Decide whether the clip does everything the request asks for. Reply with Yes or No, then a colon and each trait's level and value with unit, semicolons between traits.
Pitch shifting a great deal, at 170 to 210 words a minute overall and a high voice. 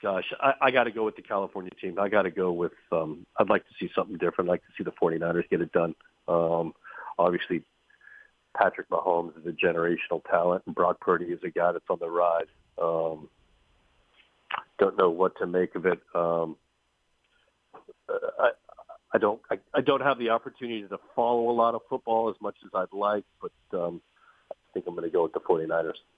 No: wide, 6.9 semitones; fast, 205 wpm; low, 110 Hz